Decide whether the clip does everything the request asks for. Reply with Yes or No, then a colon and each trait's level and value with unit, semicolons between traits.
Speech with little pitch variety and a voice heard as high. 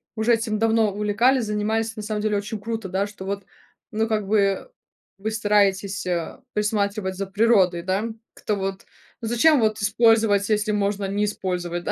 Yes: narrow, 1.9 semitones; high, 210 Hz